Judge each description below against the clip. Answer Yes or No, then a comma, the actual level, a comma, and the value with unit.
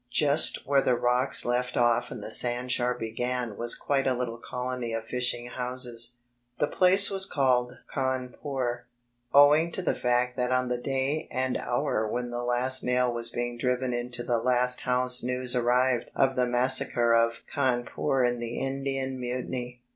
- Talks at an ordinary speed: Yes, average, 170 wpm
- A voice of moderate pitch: No, low, 125 Hz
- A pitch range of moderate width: No, narrow, 1.3 semitones